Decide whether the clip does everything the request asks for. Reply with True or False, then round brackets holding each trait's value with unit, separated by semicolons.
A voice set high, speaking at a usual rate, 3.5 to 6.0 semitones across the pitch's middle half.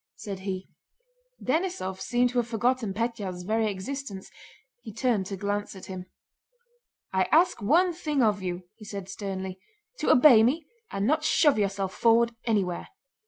True (215 Hz; 155 wpm; 4.5 semitones)